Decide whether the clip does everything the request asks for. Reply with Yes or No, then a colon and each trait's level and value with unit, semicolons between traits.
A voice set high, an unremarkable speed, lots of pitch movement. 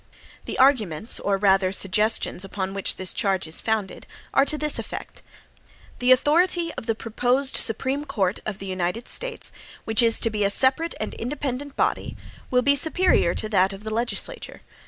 Yes: high, 225 Hz; average, 175 wpm; wide, 5.7 semitones